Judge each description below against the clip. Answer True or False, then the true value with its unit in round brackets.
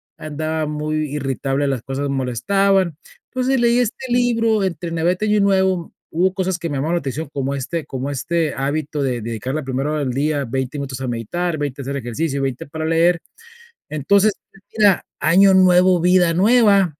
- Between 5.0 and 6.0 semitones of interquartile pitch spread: True (5.3 semitones)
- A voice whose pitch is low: False (155 Hz)